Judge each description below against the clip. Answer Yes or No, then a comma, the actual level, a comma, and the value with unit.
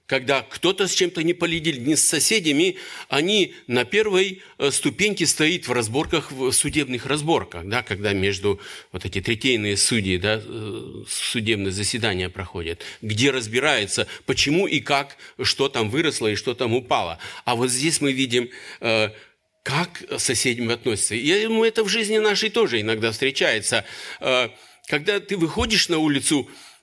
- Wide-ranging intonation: Yes, wide, 7.1 semitones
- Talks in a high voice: No, low, 135 Hz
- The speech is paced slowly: No, average, 145 wpm